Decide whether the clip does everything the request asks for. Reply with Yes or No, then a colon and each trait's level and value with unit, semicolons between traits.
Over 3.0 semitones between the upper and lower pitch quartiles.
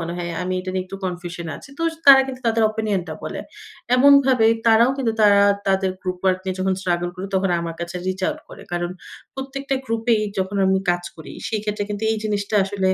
Yes: average, 3.7 semitones